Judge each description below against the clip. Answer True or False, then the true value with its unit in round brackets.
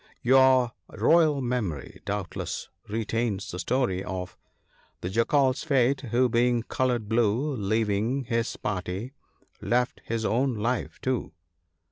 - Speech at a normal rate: False (120 wpm)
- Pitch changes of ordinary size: True (3.7 semitones)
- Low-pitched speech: True (120 Hz)